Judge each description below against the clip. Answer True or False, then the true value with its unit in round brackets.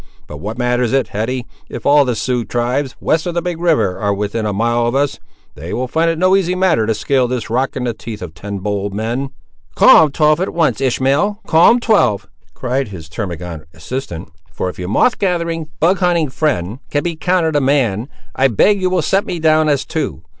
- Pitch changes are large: True (7.0 semitones)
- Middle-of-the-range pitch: False (130 Hz)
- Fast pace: True (220 wpm)